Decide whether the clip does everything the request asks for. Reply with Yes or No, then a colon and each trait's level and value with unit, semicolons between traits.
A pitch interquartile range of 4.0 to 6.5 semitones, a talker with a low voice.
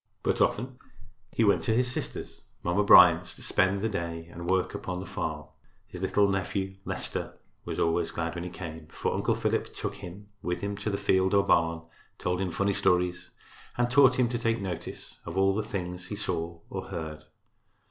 No: average, 2.9 semitones; very low, 95 Hz